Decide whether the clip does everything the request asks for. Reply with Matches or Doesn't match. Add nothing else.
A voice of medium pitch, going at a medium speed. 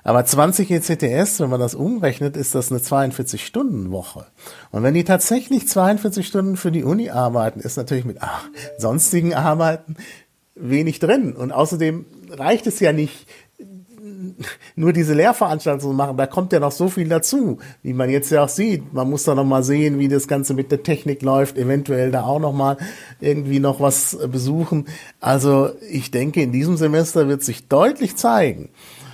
Matches